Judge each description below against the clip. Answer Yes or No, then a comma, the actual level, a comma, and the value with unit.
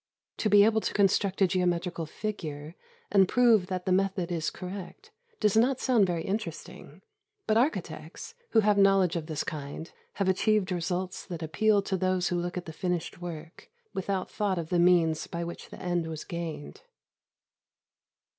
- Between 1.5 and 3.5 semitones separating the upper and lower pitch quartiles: Yes, average, 2.9 semitones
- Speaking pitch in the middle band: Yes, medium, 180 Hz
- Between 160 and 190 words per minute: Yes, average, 170 wpm